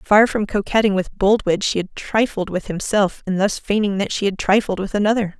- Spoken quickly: Yes, fast, 210 wpm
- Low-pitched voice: No, high, 200 Hz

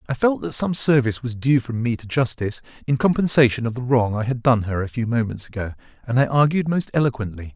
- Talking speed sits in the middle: No, fast, 230 wpm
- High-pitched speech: No, low, 125 Hz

